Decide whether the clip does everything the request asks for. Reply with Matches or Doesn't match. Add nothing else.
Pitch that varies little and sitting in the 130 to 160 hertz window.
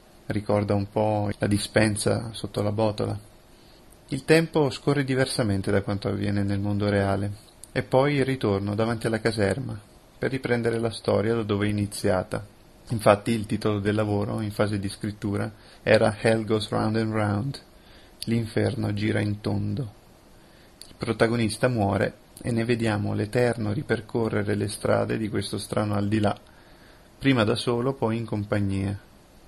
Doesn't match